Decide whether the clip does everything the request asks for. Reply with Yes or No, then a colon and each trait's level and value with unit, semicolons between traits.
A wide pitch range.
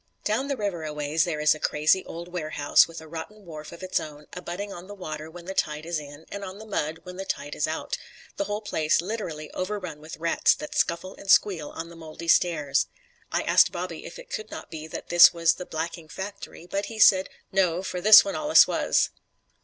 No: average, 3.8 semitones